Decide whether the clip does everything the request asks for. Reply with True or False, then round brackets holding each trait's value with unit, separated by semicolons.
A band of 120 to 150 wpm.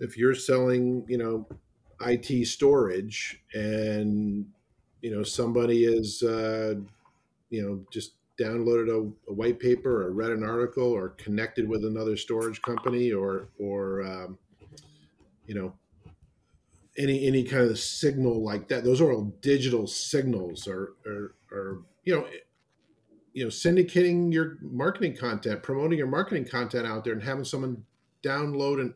True (145 wpm)